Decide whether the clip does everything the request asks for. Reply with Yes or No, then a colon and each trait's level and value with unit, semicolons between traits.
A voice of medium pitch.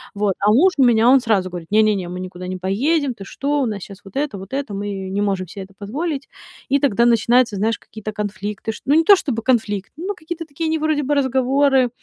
No: high, 230 Hz